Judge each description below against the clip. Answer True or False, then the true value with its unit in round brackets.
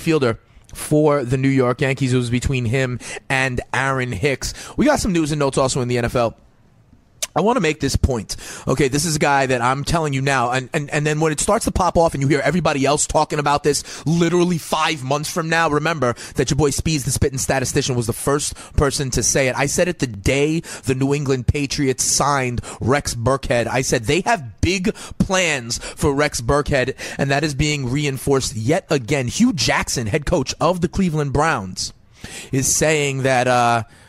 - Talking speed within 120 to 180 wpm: False (205 wpm)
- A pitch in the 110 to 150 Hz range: True (140 Hz)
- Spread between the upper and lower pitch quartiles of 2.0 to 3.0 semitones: False (3.4 semitones)